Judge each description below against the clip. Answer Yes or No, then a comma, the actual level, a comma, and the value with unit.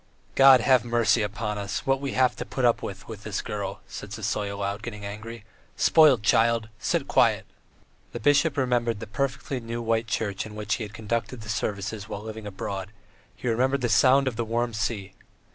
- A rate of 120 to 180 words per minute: No, average, 195 wpm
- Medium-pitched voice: No, low, 110 Hz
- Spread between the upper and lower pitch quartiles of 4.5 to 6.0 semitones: No, average, 2.8 semitones